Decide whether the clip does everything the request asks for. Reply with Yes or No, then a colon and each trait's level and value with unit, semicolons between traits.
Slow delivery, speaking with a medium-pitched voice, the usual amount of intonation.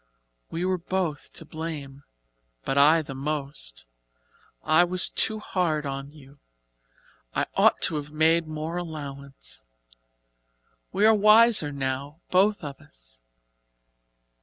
Yes: slow, 120 wpm; medium, 155 Hz; average, 4.0 semitones